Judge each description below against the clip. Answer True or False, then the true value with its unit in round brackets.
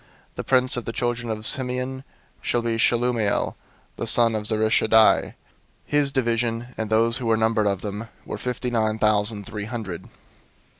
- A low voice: True (115 Hz)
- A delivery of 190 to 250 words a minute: False (165 wpm)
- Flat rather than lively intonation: True (2.0 semitones)